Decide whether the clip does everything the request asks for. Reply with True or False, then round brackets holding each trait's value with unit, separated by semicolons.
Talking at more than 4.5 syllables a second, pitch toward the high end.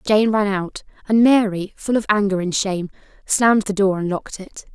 True (5.5 syllables/s; 200 Hz)